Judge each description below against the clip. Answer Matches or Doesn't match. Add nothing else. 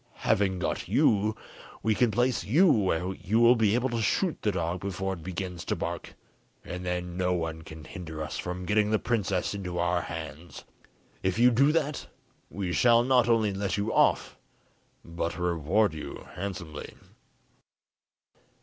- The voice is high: Doesn't match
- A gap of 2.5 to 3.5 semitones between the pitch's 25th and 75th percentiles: Doesn't match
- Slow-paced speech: Doesn't match